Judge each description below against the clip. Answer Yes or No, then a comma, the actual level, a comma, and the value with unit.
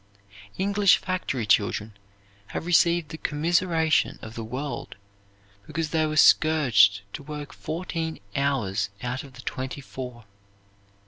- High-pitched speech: No, medium, 145 Hz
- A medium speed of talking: No, slow, 125 wpm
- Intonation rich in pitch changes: No, average, 4.7 semitones